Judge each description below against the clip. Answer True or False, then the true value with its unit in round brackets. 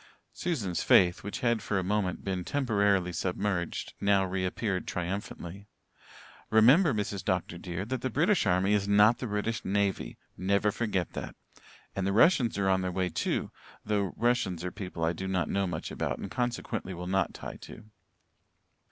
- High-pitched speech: False (100 Hz)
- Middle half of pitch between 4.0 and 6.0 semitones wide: False (2.7 semitones)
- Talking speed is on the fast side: False (170 wpm)